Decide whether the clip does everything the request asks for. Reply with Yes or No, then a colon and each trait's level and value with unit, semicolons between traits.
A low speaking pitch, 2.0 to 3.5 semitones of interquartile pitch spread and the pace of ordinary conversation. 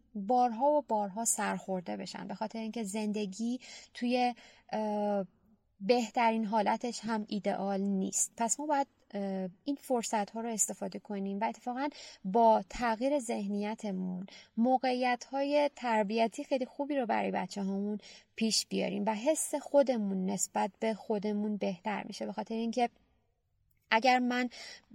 No: high, 225 Hz; average, 3.2 semitones; average, 125 wpm